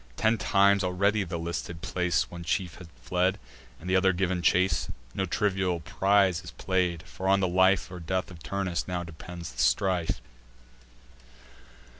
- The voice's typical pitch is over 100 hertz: No, very low, 90 Hz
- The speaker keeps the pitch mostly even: Yes, narrow, 1.8 semitones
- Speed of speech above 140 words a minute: Yes, average, 170 wpm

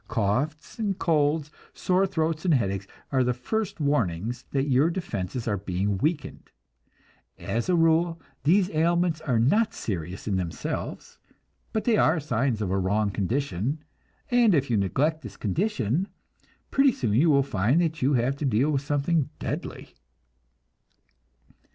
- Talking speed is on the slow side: No, average, 150 wpm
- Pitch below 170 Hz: Yes, medium, 140 Hz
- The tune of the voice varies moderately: No, wide, 7.1 semitones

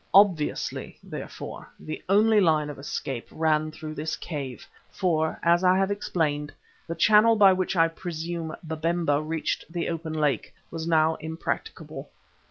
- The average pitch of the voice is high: No, medium, 160 Hz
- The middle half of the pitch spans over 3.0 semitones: No, narrow, 2.5 semitones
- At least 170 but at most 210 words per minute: No, average, 145 wpm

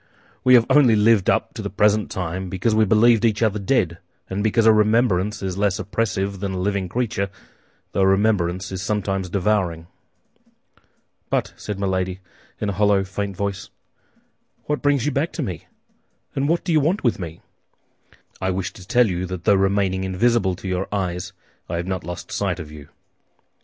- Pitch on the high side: No, low, 100 Hz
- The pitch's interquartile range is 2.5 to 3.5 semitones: Yes, average, 2.9 semitones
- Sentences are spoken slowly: No, average, 185 wpm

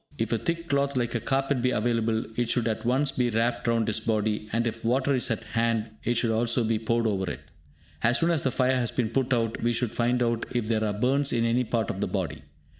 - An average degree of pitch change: No, narrow, 2.0 semitones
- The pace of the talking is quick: Yes, fast, 255 wpm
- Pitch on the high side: No, low, 120 Hz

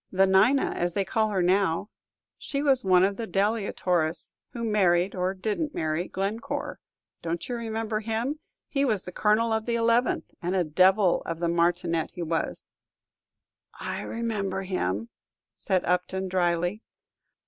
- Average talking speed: Yes, average, 150 wpm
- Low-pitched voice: No, high, 195 Hz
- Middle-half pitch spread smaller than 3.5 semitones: No, average, 4.1 semitones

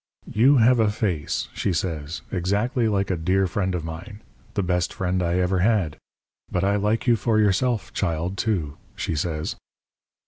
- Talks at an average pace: Yes, average, 170 wpm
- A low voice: Yes, very low, 95 Hz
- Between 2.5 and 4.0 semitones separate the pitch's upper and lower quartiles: Yes, average, 3.6 semitones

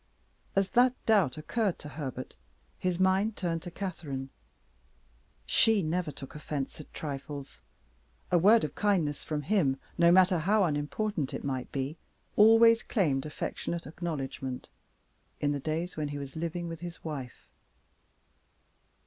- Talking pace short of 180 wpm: Yes, average, 140 wpm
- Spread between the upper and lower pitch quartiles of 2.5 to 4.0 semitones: No, average, 4.7 semitones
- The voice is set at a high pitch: No, medium, 165 Hz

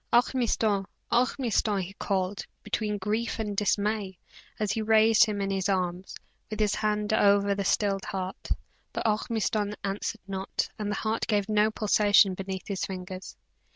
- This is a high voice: Yes, high, 205 Hz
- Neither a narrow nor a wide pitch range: No, narrow, 1.9 semitones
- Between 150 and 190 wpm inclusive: Yes, average, 155 wpm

